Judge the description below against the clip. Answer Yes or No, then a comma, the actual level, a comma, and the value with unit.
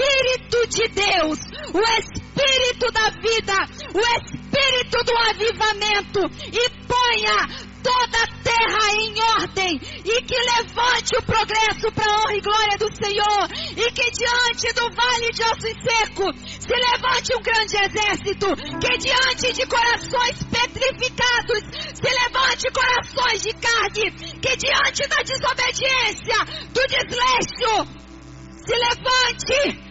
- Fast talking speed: No, slow, 120 wpm